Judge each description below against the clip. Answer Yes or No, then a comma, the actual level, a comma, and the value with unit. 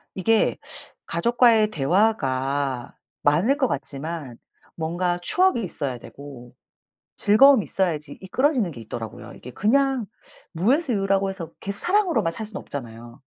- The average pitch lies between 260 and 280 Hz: No, medium, 185 Hz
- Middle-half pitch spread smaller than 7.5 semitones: No, wide, 8.2 semitones